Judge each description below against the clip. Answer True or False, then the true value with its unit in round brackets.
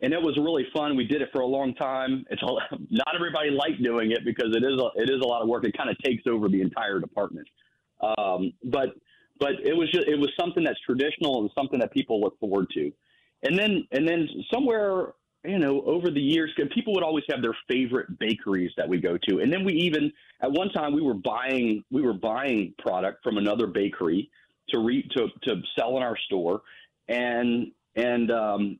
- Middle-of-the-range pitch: True (145 Hz)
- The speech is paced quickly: True (215 wpm)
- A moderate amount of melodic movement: False (8.3 semitones)